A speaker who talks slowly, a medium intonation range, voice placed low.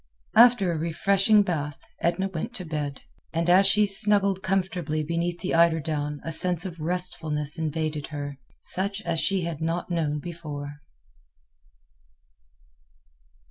No: slow, 130 wpm; average, 3.6 semitones; medium, 170 Hz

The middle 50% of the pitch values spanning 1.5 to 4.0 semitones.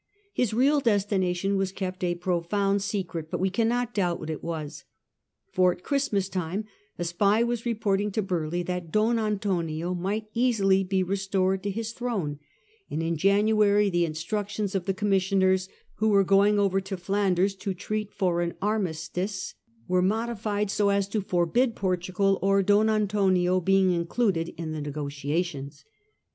Yes: average, 2.8 semitones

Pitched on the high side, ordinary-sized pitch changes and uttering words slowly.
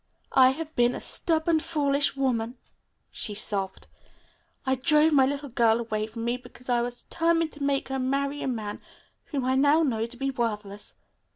No: very high, 260 Hz; average, 3.6 semitones; average, 180 wpm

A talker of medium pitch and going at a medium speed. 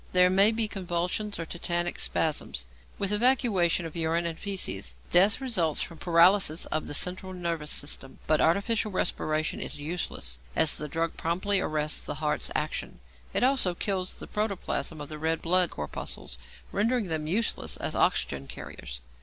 Yes: medium, 170 Hz; average, 160 wpm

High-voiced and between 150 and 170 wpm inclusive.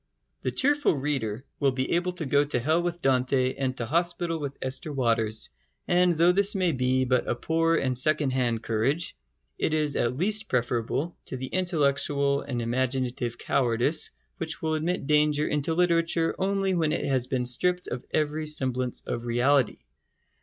No: medium, 140 Hz; average, 165 wpm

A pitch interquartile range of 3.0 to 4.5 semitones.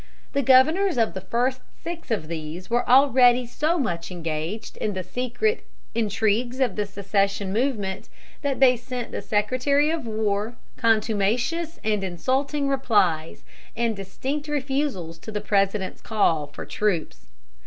No: average, 5.2 semitones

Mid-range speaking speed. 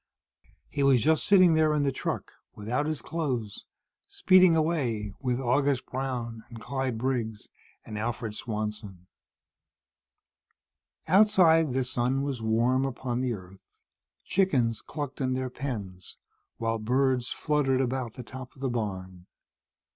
No: slow, 130 wpm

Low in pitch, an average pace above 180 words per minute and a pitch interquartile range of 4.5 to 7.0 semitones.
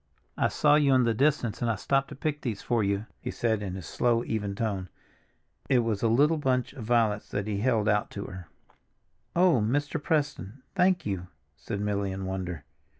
Yes: low, 115 Hz; average, 200 wpm; average, 5.3 semitones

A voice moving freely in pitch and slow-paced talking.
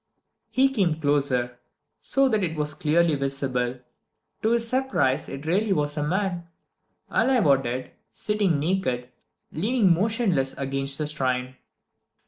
Yes: wide, 6.8 semitones; slow, 130 wpm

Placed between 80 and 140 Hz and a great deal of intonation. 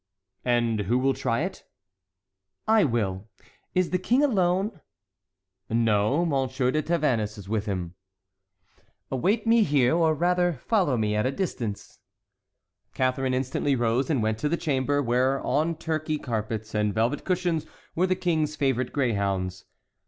Yes: low, 135 Hz; wide, 6.8 semitones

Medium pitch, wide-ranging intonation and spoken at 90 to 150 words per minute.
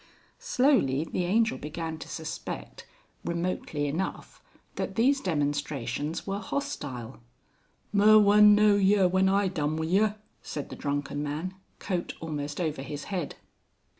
Yes: medium, 170 Hz; wide, 5.7 semitones; slow, 135 wpm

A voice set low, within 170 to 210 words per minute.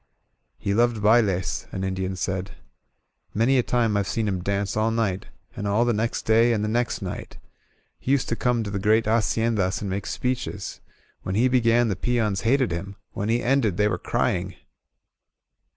Yes: low, 110 Hz; average, 190 wpm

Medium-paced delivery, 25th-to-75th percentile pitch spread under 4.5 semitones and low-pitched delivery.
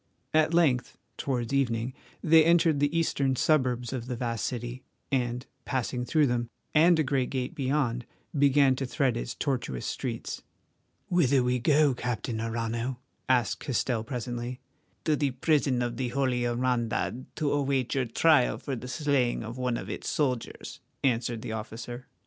Yes: average, 155 wpm; average, 2.8 semitones; low, 125 Hz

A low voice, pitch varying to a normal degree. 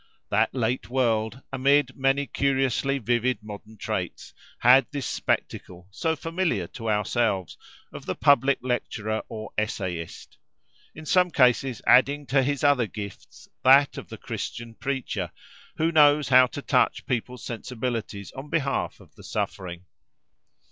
Yes: low, 125 Hz; average, 4.1 semitones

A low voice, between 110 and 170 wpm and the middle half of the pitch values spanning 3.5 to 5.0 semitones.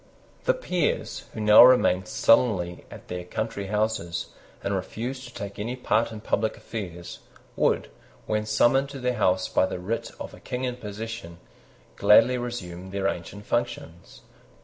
Yes: low, 110 Hz; average, 155 wpm; average, 4.4 semitones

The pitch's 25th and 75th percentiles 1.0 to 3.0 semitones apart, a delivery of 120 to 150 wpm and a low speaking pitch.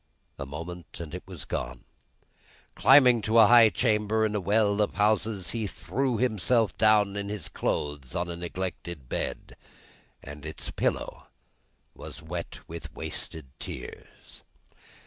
No: average, 4.5 semitones; average, 140 wpm; low, 100 Hz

